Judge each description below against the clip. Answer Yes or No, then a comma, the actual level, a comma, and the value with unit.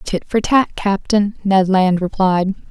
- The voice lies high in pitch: Yes, high, 195 Hz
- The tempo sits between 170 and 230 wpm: No, average, 155 wpm